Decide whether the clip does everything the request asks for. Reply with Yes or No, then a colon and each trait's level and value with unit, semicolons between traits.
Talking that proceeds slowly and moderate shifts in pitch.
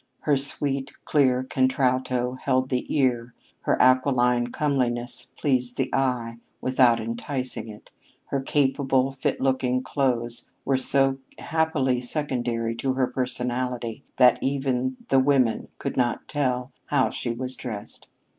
No: slow, 125 wpm; narrow, 1.6 semitones